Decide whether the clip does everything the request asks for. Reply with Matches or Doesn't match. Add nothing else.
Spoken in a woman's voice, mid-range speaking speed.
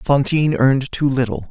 Doesn't match